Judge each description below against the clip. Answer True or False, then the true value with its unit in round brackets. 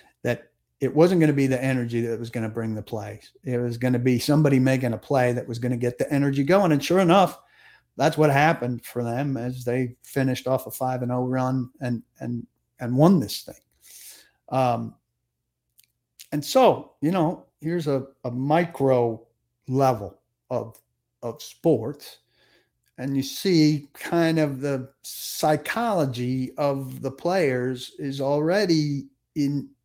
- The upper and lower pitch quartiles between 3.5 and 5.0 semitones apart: False (3.1 semitones)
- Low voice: True (130 Hz)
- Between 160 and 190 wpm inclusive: True (165 wpm)